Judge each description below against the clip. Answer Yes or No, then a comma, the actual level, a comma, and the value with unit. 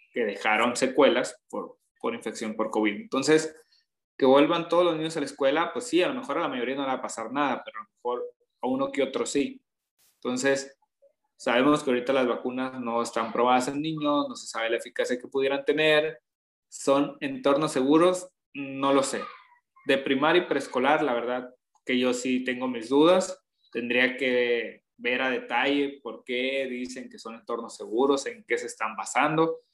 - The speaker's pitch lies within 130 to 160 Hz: Yes, medium, 140 Hz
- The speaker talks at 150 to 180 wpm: No, fast, 190 wpm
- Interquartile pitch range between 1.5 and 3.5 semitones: No, average, 3.9 semitones